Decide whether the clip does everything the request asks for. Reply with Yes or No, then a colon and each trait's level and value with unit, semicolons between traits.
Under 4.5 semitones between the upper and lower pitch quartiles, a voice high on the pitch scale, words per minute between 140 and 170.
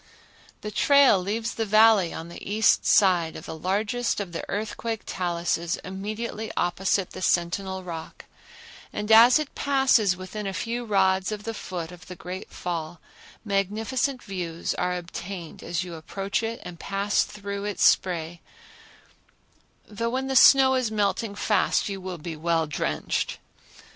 Yes: average, 3.8 semitones; high, 195 Hz; average, 155 wpm